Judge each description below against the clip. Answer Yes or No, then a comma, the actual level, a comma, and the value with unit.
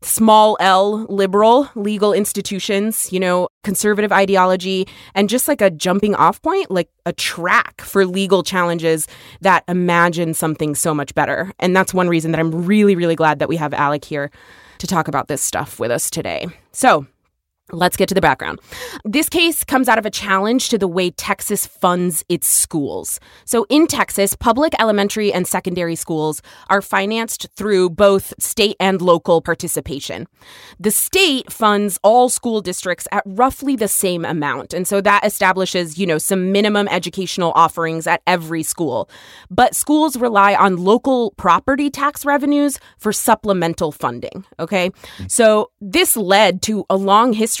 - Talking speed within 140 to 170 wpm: Yes, average, 165 wpm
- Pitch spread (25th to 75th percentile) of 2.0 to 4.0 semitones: Yes, average, 3.7 semitones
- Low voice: No, high, 195 Hz